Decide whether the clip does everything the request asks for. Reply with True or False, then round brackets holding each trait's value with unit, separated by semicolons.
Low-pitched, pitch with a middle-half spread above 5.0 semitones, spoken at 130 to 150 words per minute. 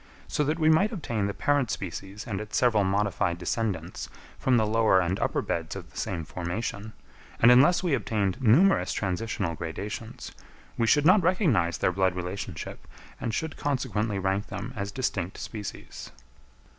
False (105 Hz; 5.4 semitones; 160 wpm)